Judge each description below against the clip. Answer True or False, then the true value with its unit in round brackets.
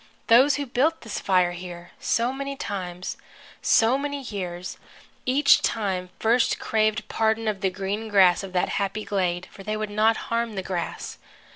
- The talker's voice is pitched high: True (215 Hz)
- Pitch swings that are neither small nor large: True (3.8 semitones)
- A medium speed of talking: True (165 wpm)